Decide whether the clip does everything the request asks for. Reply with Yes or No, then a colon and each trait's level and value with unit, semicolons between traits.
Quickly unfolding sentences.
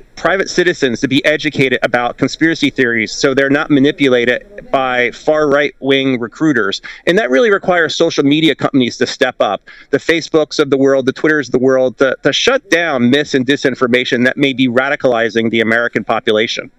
No: average, 180 wpm